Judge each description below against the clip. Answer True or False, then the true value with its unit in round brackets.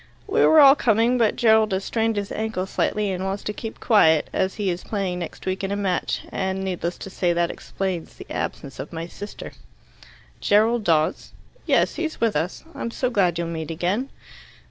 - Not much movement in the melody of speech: False (4.0 semitones)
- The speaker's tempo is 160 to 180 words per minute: False (195 wpm)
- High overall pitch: True (195 Hz)